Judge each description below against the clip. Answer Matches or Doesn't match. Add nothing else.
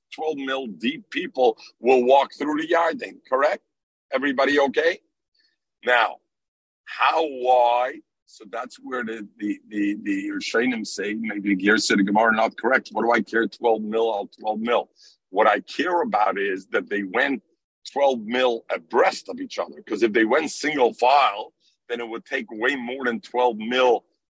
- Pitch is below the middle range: Matches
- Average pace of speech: Matches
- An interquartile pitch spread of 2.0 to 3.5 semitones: Doesn't match